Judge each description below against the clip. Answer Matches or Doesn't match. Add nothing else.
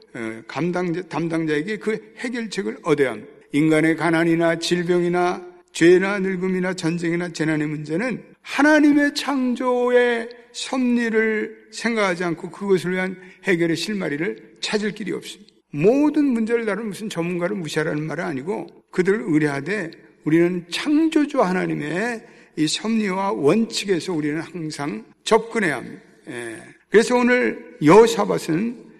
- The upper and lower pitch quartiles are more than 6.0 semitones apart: Doesn't match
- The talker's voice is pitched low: Doesn't match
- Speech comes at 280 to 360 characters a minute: Matches